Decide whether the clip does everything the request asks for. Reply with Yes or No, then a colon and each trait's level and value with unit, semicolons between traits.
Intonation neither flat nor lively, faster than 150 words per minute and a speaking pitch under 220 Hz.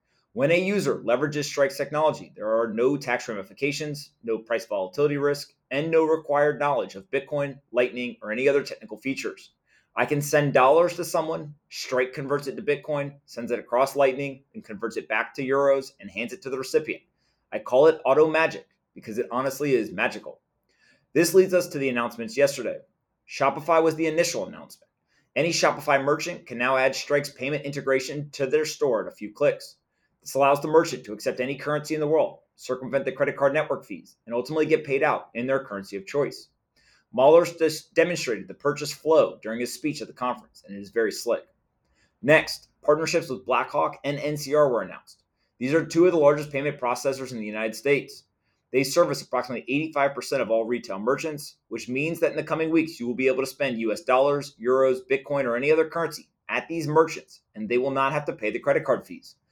Yes: average, 3.4 semitones; average, 200 wpm; medium, 140 Hz